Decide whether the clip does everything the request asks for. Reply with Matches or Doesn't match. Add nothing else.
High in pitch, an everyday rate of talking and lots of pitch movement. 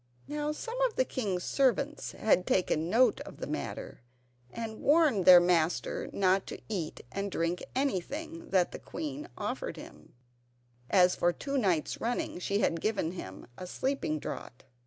Matches